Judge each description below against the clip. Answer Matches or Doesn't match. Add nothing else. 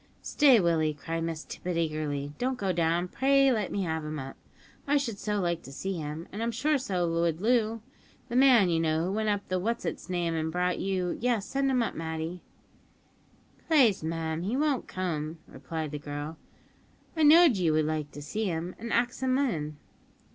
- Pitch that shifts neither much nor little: Doesn't match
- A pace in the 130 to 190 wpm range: Doesn't match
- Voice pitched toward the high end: Doesn't match